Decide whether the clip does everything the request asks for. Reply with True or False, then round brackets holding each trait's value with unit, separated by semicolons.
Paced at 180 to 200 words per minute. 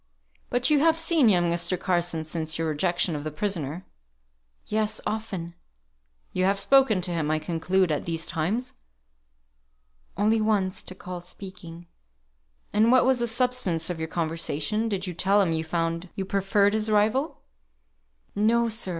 False (160 wpm)